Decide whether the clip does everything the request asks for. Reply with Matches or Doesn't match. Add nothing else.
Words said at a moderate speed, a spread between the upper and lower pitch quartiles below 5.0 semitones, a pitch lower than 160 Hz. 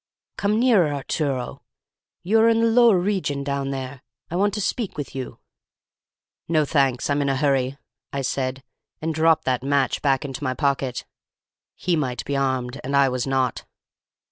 Matches